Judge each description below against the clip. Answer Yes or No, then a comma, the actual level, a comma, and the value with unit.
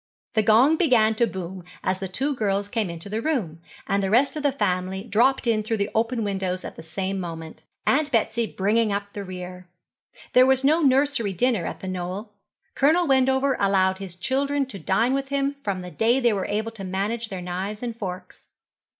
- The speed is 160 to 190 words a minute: No, average, 200 wpm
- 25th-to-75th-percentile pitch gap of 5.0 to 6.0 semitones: Yes, average, 5.3 semitones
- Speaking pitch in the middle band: No, high, 215 Hz